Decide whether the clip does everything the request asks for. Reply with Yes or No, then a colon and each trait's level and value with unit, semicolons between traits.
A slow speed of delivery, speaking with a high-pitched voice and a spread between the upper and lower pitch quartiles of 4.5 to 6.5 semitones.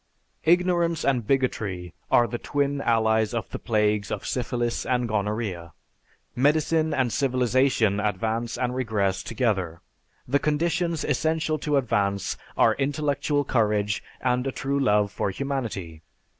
No: slow, 130 wpm; low, 120 Hz; average, 5.1 semitones